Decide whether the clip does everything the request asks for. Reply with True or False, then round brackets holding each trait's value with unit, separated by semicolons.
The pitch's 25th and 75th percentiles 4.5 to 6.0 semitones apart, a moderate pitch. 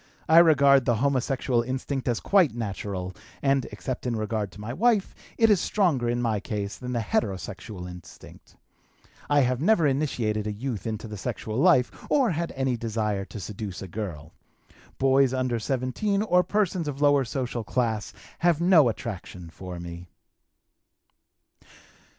False (5.2 semitones; 125 Hz)